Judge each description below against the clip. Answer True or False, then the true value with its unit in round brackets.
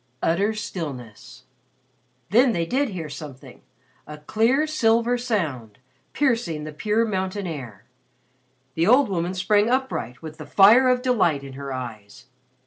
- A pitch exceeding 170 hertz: True (185 Hz)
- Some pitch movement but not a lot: False (7.6 semitones)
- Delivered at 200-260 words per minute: False (135 wpm)